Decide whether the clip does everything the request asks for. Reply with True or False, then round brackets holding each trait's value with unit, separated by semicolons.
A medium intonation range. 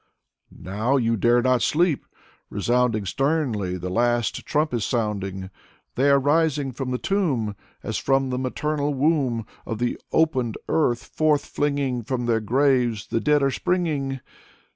True (3.9 semitones)